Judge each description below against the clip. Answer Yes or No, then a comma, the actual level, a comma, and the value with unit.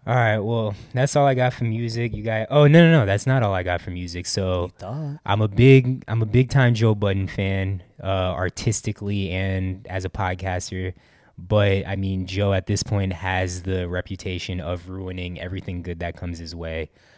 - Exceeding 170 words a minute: Yes, average, 200 wpm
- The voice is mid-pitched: No, very low, 95 Hz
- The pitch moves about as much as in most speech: Yes, average, 3.8 semitones